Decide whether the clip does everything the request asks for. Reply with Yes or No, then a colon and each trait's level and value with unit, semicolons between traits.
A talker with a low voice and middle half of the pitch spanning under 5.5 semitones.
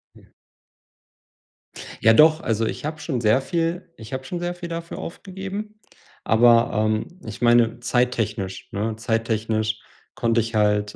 No: low, 120 Hz; wide, 7.1 semitones